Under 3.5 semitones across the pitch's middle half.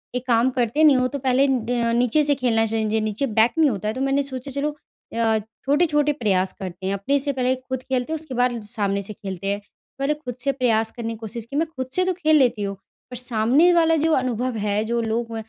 No: average, 4.0 semitones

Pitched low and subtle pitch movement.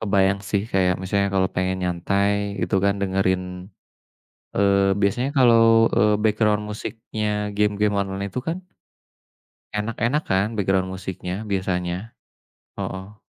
Yes: low, 100 Hz; narrow, 1.8 semitones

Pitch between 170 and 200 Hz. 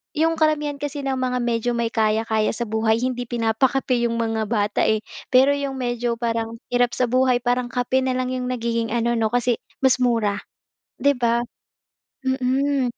No: high, 245 Hz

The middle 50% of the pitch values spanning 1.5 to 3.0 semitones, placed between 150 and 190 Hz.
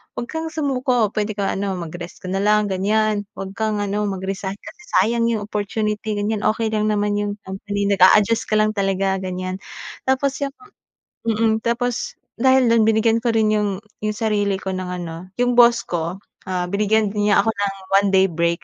No: narrow, 2.5 semitones; high, 210 Hz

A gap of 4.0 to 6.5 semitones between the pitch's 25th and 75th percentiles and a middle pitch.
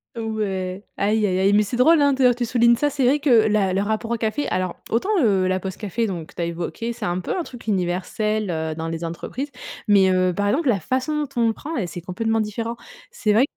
No: average, 4.5 semitones; high, 215 Hz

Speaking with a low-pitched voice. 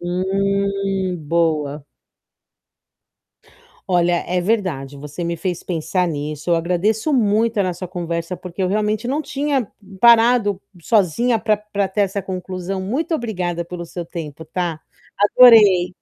No: medium, 185 Hz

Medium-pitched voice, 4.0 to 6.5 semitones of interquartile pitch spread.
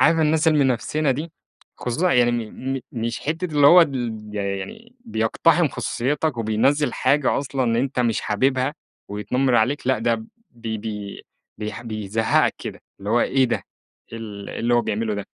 No: low, 120 Hz; average, 4.4 semitones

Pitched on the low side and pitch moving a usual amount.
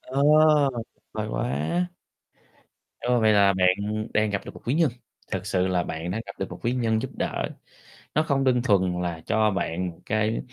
Yes: low, 105 Hz; average, 4.5 semitones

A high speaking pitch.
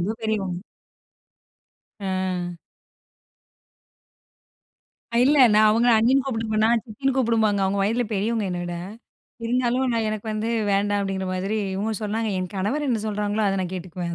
Yes: high, 215 Hz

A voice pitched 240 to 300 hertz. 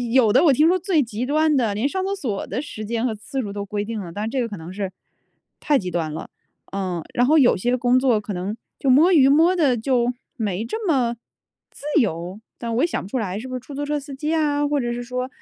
Yes: high, 245 Hz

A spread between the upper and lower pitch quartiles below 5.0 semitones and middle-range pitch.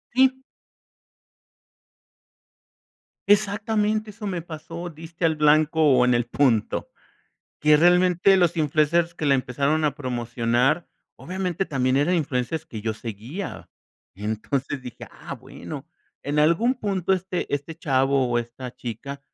No: wide, 5.5 semitones; medium, 150 Hz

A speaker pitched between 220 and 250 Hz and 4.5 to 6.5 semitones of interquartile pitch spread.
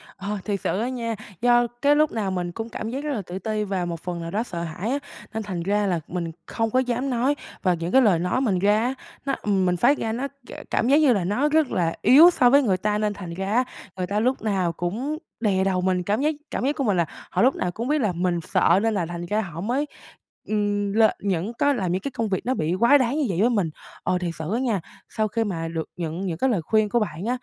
No: high, 210 Hz; average, 5.2 semitones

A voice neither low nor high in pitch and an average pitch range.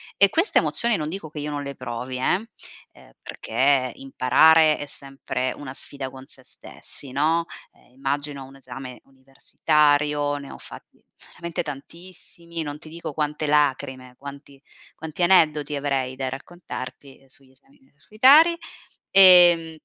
Yes: medium, 145 Hz; average, 3.3 semitones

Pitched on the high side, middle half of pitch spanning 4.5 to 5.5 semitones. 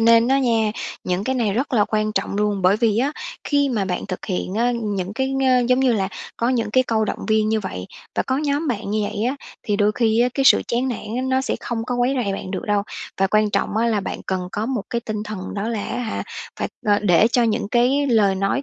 No: high, 220 Hz; average, 3.2 semitones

